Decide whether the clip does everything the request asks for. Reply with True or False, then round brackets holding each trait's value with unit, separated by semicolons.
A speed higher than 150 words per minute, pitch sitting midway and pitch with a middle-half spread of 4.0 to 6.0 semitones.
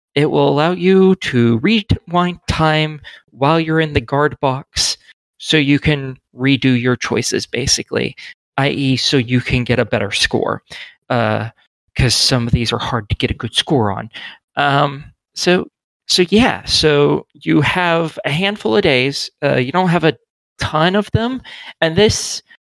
True (165 wpm; 145 Hz; 4.6 semitones)